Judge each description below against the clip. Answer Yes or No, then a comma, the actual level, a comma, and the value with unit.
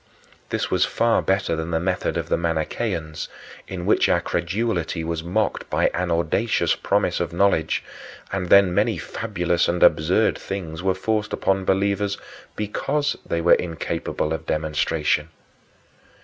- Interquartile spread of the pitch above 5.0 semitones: No, average, 3.3 semitones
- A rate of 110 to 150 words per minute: Yes, average, 145 wpm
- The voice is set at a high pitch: No, very low, 90 Hz